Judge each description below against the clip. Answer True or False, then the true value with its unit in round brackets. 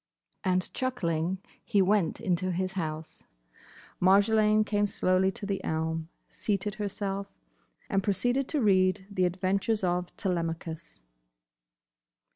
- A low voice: False (190 Hz)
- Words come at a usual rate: False (110 wpm)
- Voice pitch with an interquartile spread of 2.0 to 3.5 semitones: True (2.6 semitones)